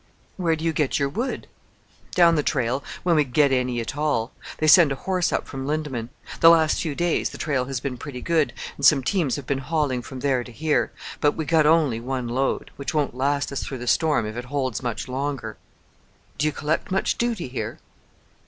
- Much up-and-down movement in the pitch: No, average, 3.5 semitones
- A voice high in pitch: No, medium, 140 Hz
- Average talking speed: No, fast, 215 wpm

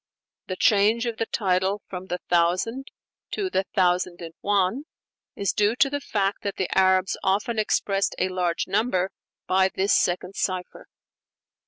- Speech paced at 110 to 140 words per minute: No, average, 155 wpm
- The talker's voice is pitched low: No, high, 195 Hz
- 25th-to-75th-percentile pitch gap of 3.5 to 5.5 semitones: No, narrow, 2.6 semitones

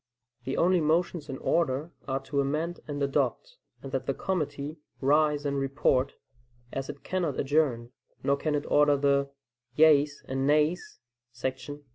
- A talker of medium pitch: Yes, medium, 145 Hz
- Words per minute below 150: No, average, 155 wpm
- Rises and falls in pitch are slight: Yes, narrow, 2.1 semitones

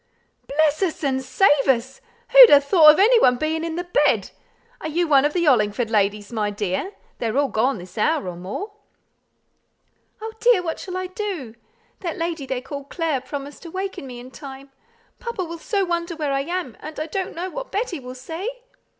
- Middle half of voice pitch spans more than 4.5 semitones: Yes, wide, 5.6 semitones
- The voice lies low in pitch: No, very high, 305 Hz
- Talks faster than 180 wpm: Yes, average, 200 wpm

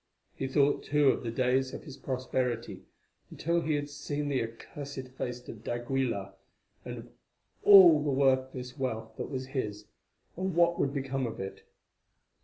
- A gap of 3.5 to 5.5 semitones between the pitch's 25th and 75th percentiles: No, average, 2.8 semitones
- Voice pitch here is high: No, low, 130 Hz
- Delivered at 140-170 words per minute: Yes, average, 160 wpm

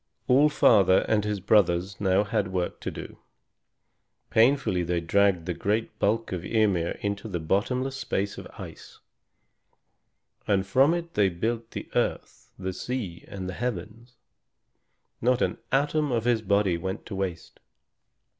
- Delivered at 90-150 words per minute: Yes, average, 145 wpm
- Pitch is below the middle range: Yes, low, 100 Hz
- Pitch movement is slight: No, average, 4.1 semitones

